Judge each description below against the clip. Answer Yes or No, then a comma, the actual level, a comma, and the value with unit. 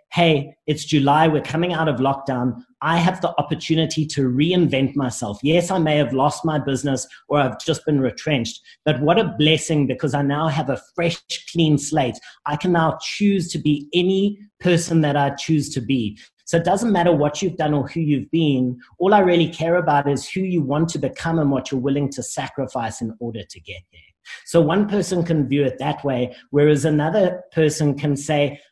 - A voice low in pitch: No, medium, 150 Hz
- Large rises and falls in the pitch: No, average, 3.3 semitones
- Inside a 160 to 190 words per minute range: No, fast, 205 wpm